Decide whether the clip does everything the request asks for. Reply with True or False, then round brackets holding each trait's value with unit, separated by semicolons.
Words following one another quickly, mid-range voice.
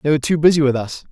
True (325 wpm; 145 Hz)